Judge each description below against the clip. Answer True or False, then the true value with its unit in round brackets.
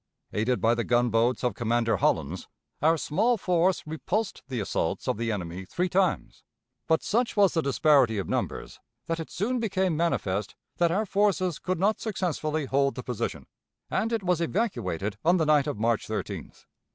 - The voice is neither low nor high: True (155 Hz)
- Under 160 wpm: False (175 wpm)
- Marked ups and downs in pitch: True (8.2 semitones)